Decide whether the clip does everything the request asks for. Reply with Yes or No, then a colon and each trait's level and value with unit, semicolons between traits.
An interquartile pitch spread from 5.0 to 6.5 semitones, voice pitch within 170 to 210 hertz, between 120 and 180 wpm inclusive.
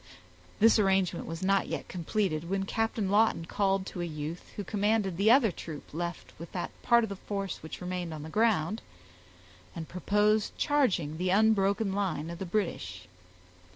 No: average, 3.8 semitones; high, 190 Hz; average, 170 wpm